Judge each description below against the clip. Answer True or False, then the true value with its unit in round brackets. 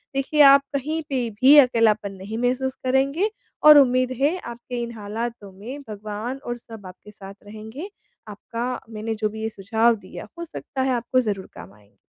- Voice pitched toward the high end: True (235 Hz)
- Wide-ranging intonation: False (3.8 semitones)